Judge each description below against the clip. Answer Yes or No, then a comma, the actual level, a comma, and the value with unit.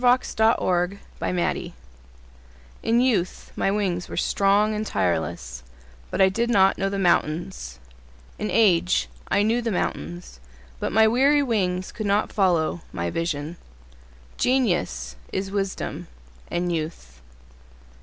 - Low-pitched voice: No, high, 190 Hz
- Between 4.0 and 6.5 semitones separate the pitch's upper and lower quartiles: Yes, average, 4.4 semitones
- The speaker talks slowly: Yes, slow, 125 wpm